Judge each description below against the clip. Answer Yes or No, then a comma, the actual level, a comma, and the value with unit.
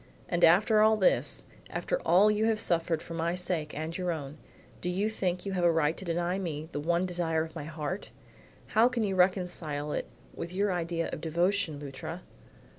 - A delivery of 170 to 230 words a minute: Yes, average, 195 wpm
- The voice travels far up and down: No, average, 2.8 semitones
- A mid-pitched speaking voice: Yes, medium, 175 Hz